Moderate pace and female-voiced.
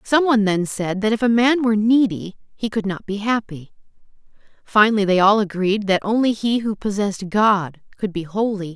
Yes: average, 190 wpm; female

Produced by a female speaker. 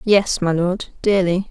Yes: female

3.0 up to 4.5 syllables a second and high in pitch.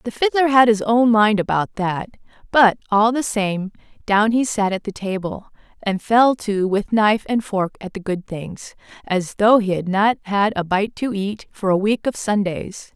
Yes: 4.4 syllables/s; high, 210 Hz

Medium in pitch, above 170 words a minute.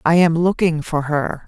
Yes: medium, 160 Hz; fast, 205 wpm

